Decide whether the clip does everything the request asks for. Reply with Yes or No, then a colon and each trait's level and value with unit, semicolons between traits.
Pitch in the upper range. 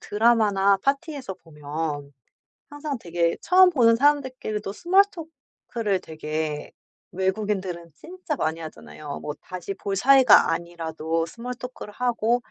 Yes: high, 205 Hz